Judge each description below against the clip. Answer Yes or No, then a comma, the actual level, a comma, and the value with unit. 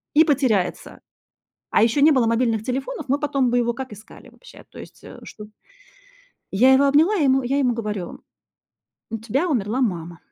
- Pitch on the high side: Yes, very high, 250 Hz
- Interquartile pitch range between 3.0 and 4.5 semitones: Yes, average, 4.2 semitones